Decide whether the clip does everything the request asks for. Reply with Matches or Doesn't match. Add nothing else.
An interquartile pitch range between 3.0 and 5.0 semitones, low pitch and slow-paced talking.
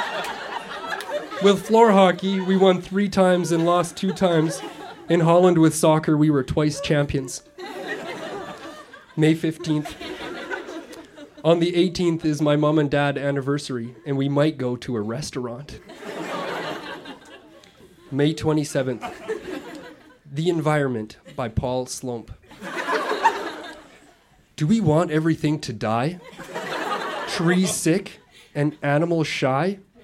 Doesn't match